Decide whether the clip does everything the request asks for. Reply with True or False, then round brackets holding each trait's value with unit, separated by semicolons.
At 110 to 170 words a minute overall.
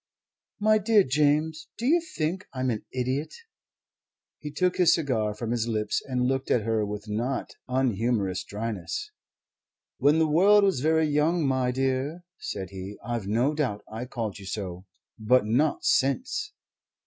True (155 wpm)